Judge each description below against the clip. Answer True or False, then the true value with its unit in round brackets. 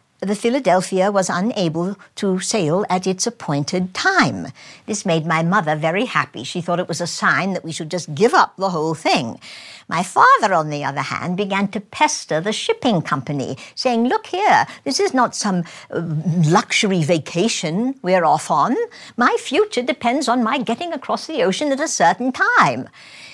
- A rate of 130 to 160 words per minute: False (175 wpm)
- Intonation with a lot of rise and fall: True (5.8 semitones)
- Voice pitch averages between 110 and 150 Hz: False (190 Hz)